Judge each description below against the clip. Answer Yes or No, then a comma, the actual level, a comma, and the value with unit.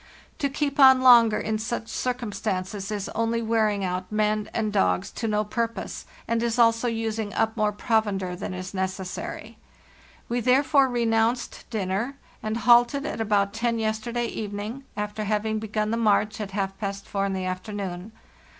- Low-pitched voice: No, high, 220 Hz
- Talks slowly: No, average, 170 wpm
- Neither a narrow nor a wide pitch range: No, narrow, 2.3 semitones